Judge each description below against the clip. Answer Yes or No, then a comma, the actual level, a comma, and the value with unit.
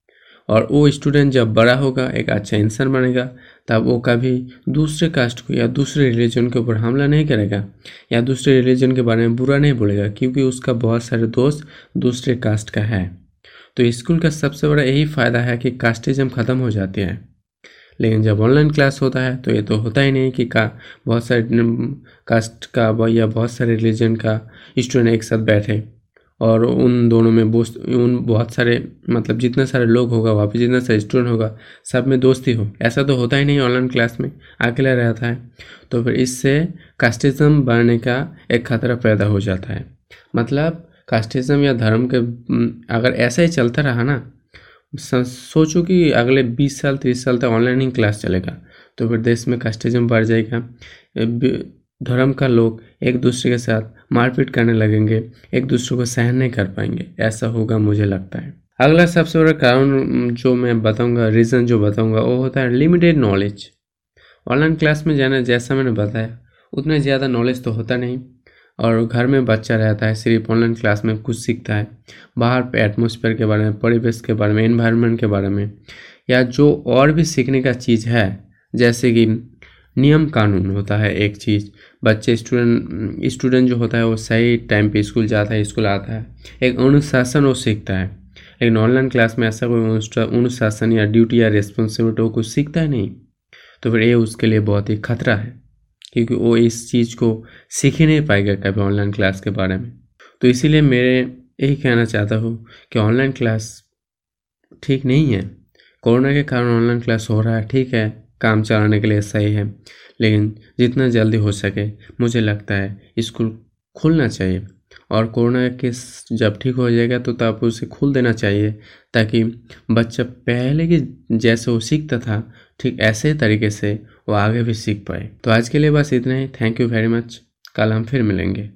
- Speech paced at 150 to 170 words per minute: No, average, 185 wpm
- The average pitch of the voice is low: Yes, low, 120 Hz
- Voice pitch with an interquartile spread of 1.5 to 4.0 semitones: Yes, narrow, 2.5 semitones